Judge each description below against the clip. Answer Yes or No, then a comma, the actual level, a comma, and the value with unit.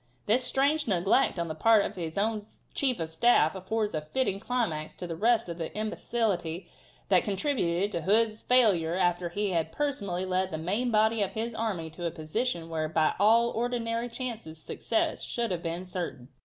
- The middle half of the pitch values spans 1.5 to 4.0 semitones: No, average, 5.3 semitones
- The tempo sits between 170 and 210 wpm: Yes, average, 190 wpm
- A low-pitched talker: No, high, 195 Hz